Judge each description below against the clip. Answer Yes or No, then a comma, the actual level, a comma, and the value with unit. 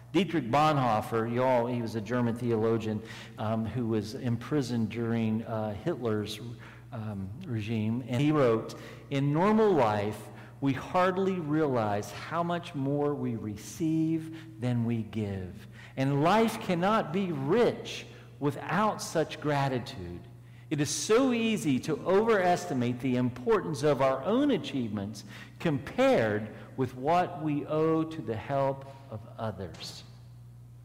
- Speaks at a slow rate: Yes, slow, 125 wpm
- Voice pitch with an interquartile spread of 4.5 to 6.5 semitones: Yes, wide, 5.4 semitones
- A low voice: Yes, low, 125 Hz